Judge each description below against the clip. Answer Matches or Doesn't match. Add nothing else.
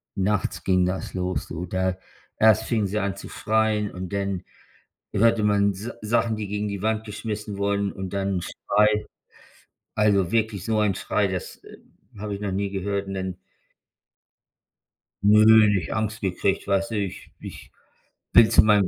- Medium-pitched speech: Doesn't match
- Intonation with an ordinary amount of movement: Doesn't match